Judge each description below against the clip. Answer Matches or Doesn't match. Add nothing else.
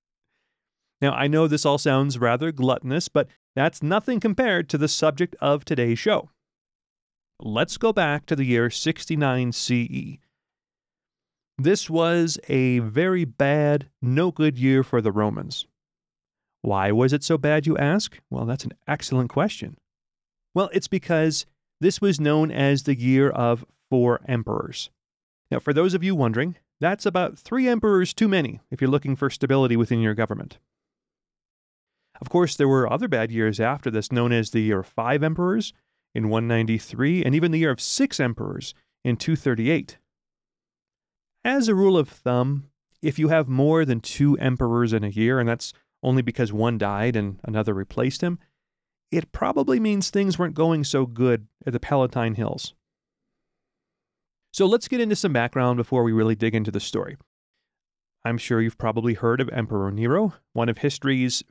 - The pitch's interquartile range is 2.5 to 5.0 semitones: Doesn't match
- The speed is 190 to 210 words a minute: Doesn't match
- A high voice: Doesn't match